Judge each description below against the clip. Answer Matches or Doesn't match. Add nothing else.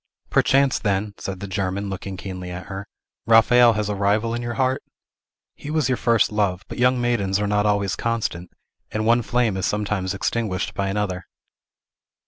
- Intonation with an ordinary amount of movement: Matches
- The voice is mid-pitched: Doesn't match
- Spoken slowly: Doesn't match